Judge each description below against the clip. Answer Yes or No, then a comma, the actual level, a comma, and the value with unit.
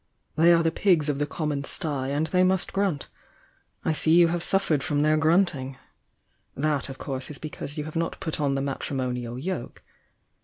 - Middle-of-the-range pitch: Yes, medium, 150 Hz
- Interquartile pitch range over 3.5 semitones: No, average, 3.2 semitones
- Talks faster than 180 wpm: Yes, average, 190 wpm